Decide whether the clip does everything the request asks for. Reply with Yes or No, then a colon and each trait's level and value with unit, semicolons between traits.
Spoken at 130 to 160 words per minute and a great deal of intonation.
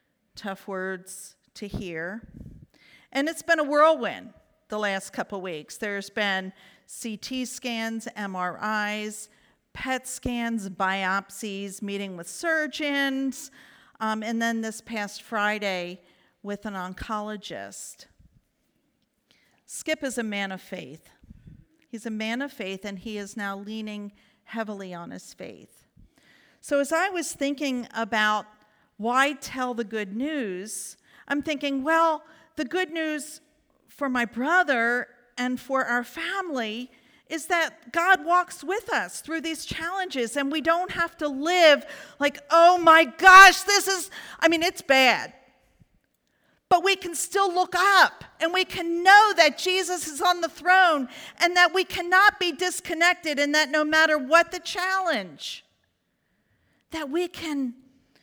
Yes: average, 140 wpm; wide, 7.5 semitones